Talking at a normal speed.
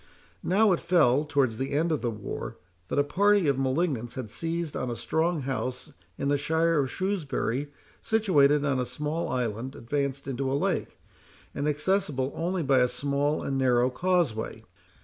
Yes: average, 170 wpm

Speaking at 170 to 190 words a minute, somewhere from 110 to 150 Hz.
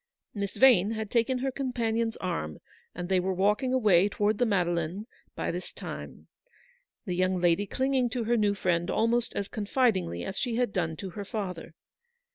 No: average, 180 wpm; high, 205 Hz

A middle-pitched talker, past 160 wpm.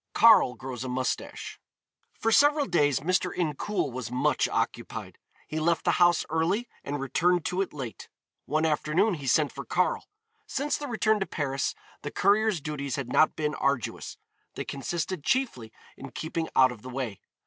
Yes: medium, 155 Hz; average, 170 wpm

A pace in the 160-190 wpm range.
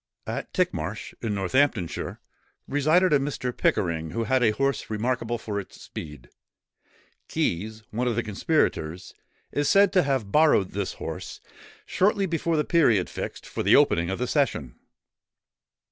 No: average, 145 wpm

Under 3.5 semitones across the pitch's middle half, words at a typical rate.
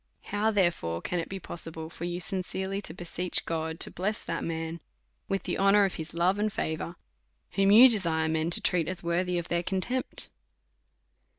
Yes: average, 2.9 semitones; average, 195 wpm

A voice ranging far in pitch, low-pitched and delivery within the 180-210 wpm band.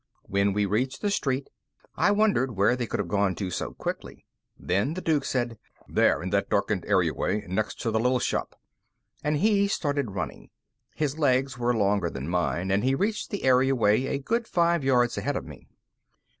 Yes: wide, 6.1 semitones; low, 125 Hz; average, 195 wpm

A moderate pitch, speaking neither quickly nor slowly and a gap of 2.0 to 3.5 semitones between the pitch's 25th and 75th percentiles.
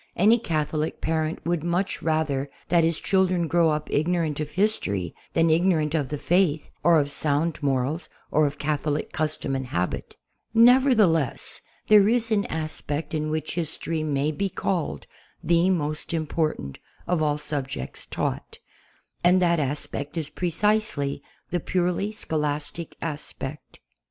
Yes: medium, 160 Hz; average, 145 wpm; average, 3.0 semitones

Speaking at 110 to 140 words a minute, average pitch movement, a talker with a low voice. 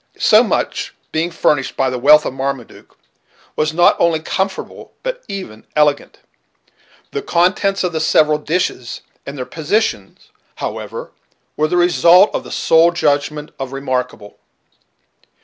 No: slow, 135 wpm; average, 4.3 semitones; medium, 155 Hz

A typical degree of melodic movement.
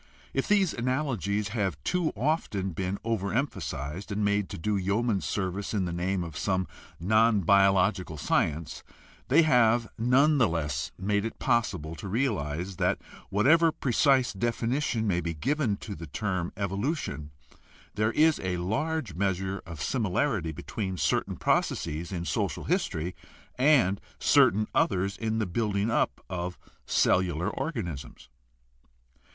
Yes: average, 4.8 semitones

